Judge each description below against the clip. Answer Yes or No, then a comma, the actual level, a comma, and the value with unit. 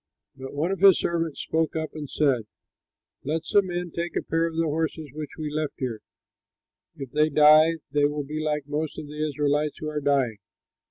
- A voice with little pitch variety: Yes, narrow, 1.8 semitones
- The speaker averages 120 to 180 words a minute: No, fast, 205 wpm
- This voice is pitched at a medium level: Yes, medium, 150 Hz